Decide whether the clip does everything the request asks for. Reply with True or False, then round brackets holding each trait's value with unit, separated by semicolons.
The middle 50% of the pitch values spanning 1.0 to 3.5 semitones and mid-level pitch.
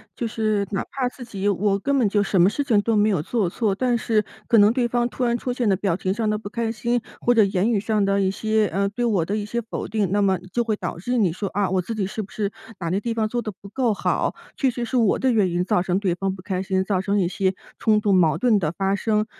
False (3.2 semitones; 210 Hz)